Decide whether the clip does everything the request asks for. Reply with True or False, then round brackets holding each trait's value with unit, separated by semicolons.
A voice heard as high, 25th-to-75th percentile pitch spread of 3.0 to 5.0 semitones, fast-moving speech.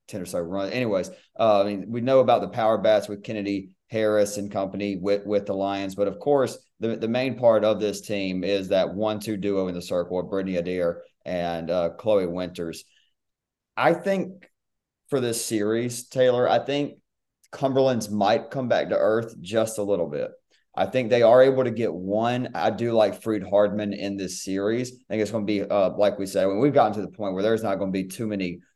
False (105 Hz; 3.5 semitones; 220 wpm)